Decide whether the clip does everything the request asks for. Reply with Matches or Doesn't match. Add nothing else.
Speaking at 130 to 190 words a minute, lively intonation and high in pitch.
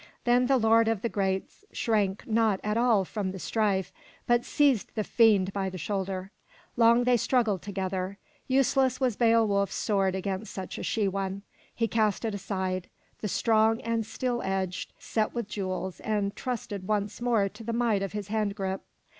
Doesn't match